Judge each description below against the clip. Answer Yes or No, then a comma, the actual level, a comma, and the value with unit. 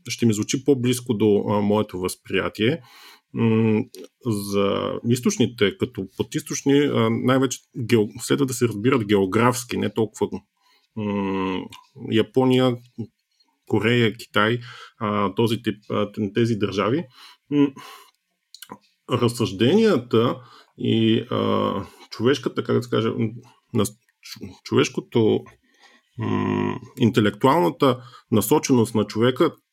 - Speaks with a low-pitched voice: Yes, low, 115 Hz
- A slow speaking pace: Yes, slow, 100 wpm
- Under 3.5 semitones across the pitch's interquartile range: Yes, average, 2.9 semitones